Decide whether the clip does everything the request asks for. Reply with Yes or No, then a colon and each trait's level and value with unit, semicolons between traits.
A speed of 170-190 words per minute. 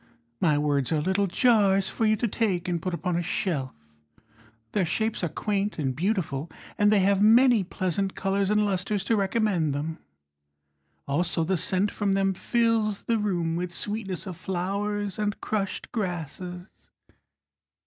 No: average, 155 wpm